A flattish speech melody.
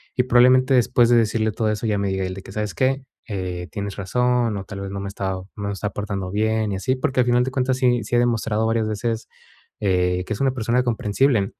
No: average, 3.7 semitones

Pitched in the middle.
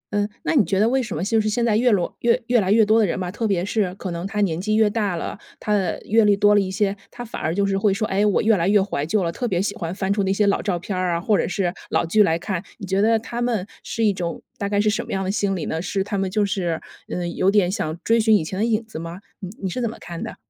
No: high, 200 Hz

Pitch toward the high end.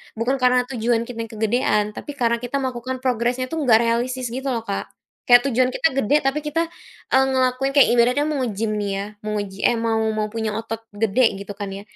Yes: high, 240 Hz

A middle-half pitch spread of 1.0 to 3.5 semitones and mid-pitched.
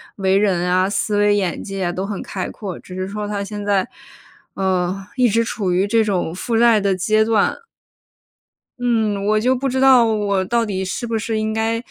No: average, 2.8 semitones; high, 205 Hz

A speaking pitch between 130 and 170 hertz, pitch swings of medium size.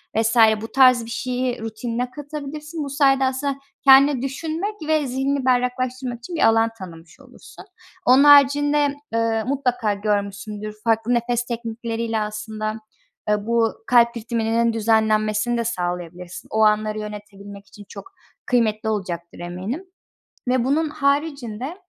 No: high, 235 Hz; average, 4.0 semitones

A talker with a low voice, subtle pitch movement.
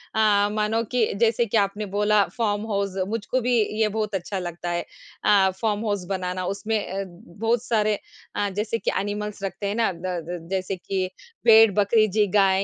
No: high, 205 Hz; narrow, 2.3 semitones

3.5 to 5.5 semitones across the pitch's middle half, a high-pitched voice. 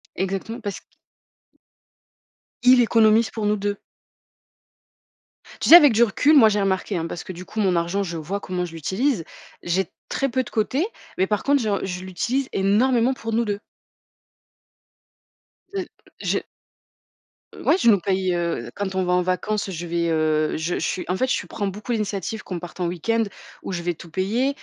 Yes: average, 4.1 semitones; high, 195 Hz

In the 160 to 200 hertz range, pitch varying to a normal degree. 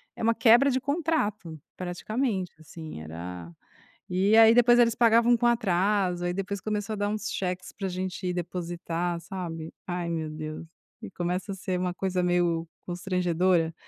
Yes: medium, 185 Hz; average, 3.7 semitones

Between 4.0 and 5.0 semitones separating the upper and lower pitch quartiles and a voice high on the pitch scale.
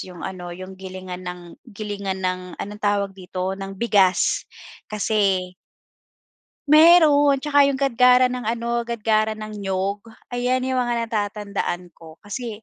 Yes: average, 4.3 semitones; high, 210 Hz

